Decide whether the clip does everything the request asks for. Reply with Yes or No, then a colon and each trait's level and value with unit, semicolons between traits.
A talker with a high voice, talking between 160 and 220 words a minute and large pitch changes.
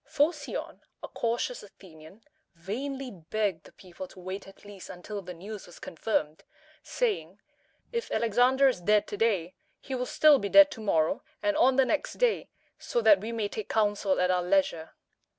Yes: high, 210 Hz; average, 175 wpm; wide, 6.1 semitones